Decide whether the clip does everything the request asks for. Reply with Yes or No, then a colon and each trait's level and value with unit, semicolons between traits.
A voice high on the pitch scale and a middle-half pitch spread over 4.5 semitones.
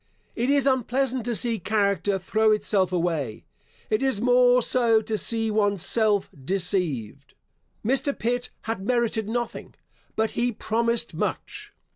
No: high, 220 Hz; average, 3.5 semitones